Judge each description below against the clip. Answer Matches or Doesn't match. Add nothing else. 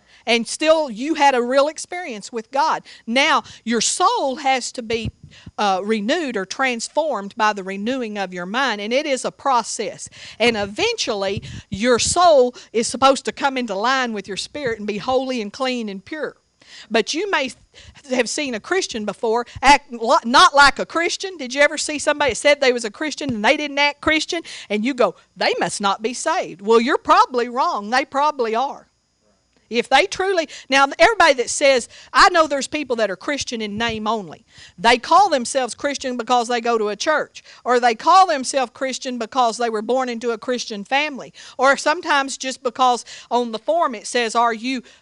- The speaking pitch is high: Matches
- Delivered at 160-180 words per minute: Doesn't match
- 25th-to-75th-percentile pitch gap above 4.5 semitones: Doesn't match